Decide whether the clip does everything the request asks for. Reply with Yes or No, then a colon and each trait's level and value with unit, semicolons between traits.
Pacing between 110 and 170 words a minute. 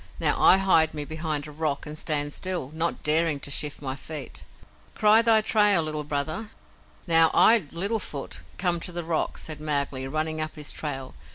No: average, 185 wpm